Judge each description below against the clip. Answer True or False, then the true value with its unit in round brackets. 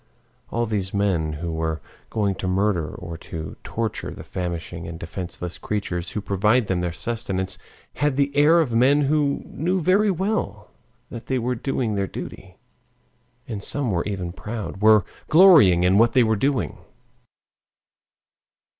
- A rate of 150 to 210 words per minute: True (155 wpm)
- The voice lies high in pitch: False (105 Hz)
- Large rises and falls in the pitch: True (6.4 semitones)